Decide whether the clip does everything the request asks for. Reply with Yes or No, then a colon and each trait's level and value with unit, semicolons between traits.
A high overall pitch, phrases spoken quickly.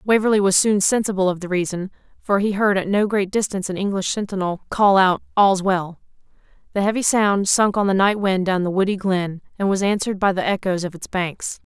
Yes: high, 195 Hz; fast, 215 wpm